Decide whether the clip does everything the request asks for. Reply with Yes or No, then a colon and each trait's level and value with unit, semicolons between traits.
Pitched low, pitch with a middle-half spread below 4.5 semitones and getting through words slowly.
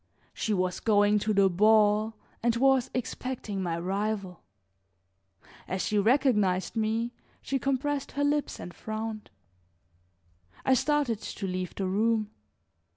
No: high, 215 Hz; average, 3.8 semitones; slow, 125 wpm